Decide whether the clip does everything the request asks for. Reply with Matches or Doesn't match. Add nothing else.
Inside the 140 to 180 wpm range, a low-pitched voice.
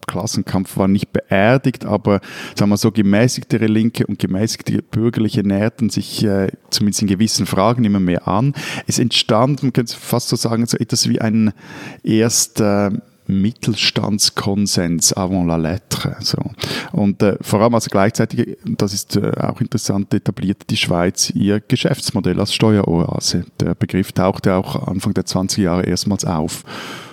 Matches